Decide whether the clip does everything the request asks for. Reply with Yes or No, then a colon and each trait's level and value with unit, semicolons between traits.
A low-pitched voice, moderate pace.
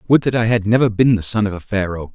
No: low, 105 Hz; fast, 305 wpm